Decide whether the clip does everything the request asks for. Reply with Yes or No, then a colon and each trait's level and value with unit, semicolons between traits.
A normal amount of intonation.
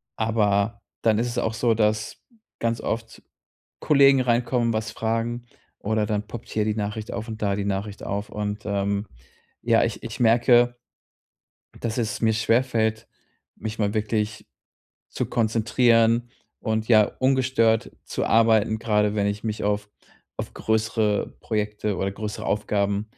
No: narrow, 1.7 semitones